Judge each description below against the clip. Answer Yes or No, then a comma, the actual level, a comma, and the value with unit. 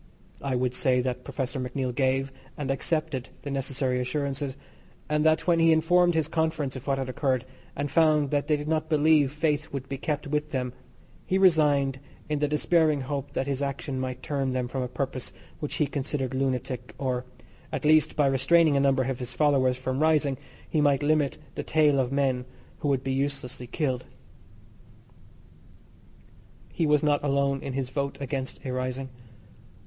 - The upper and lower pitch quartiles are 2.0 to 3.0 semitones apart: Yes, narrow, 2.4 semitones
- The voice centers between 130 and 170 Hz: Yes, medium, 140 Hz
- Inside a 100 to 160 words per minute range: No, average, 180 wpm